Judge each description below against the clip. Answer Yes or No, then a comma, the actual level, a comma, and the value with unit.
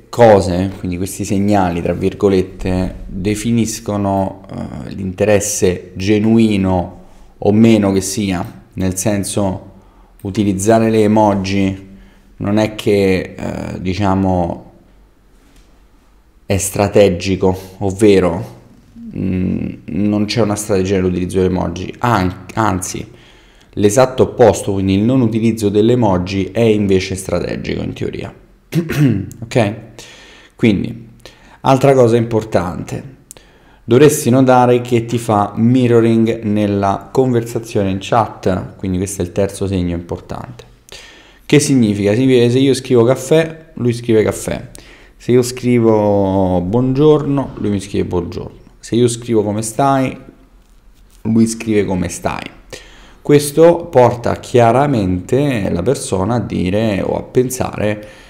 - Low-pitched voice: Yes, low, 105 Hz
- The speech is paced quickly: No, slow, 115 wpm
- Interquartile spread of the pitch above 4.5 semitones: No, average, 3.6 semitones